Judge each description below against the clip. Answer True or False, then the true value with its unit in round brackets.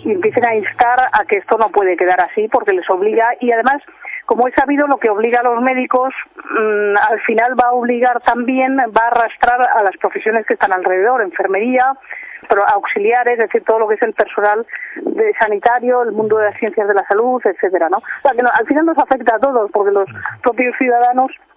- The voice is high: True (240 Hz)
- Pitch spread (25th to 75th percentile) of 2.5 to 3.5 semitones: True (3.2 semitones)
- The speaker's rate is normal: False (200 wpm)